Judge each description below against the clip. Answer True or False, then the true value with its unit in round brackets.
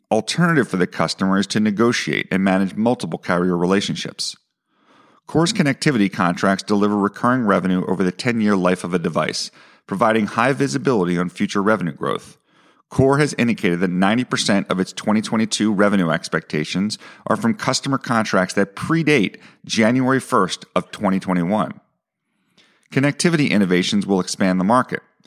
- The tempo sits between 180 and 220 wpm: False (140 wpm)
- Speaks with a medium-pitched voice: False (105 Hz)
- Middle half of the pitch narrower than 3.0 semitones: False (4.5 semitones)